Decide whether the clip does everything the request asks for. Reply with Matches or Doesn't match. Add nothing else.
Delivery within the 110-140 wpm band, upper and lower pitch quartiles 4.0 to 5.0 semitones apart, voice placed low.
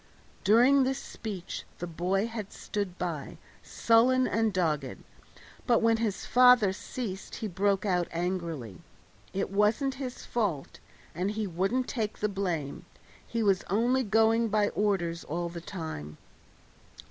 Doesn't match